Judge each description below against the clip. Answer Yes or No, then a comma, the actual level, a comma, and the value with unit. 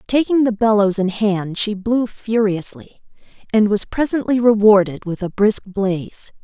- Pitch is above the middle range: Yes, high, 210 Hz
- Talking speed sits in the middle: Yes, average, 150 wpm